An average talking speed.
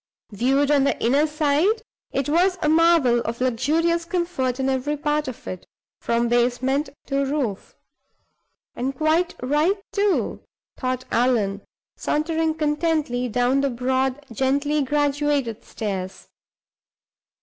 No: slow, 120 wpm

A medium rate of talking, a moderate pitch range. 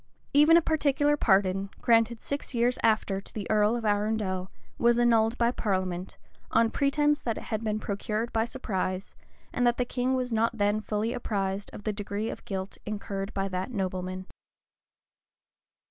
Yes: average, 165 wpm; average, 3.4 semitones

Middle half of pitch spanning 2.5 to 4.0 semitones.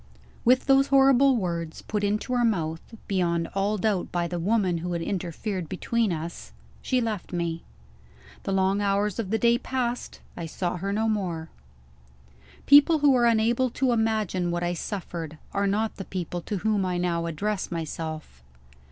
No: average, 4.6 semitones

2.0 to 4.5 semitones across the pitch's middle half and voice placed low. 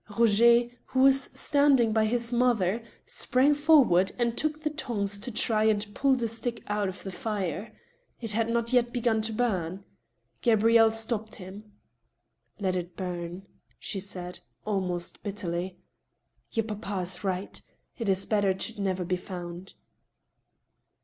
No: average, 4.0 semitones; high, 215 Hz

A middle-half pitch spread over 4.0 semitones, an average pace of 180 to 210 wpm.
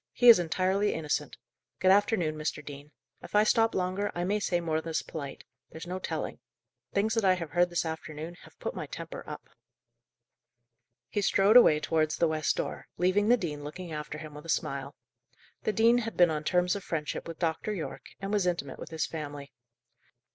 Yes: average, 4.4 semitones; average, 195 wpm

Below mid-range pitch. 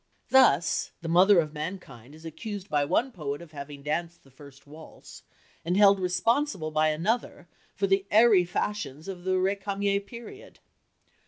No: medium, 180 Hz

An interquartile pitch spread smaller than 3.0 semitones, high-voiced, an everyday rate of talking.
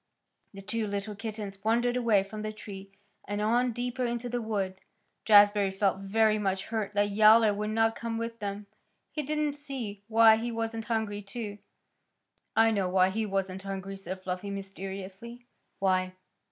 Yes: narrow, 2.5 semitones; high, 210 Hz; average, 165 wpm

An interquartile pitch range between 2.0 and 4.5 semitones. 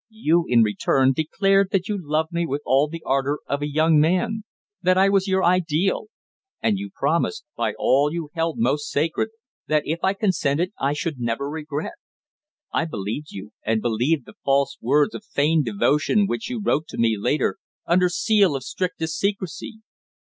No: average, 5.0 semitones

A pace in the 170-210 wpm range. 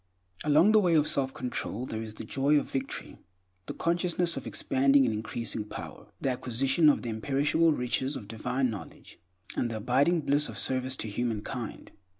Yes: average, 175 wpm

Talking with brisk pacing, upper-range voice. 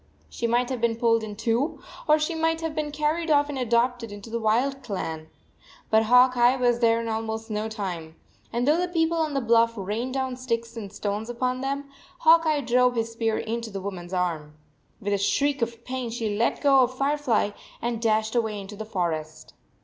Yes: fast, 210 wpm; high, 235 Hz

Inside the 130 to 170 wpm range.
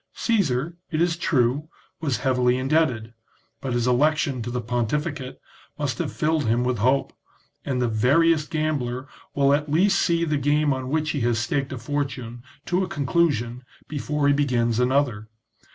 Yes: average, 165 wpm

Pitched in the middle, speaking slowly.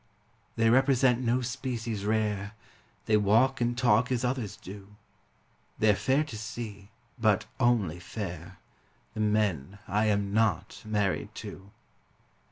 No: low, 110 Hz; slow, 125 wpm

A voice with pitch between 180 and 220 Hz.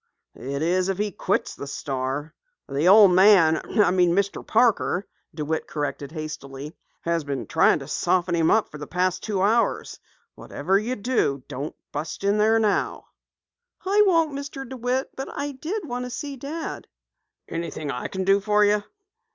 Yes: high, 190 Hz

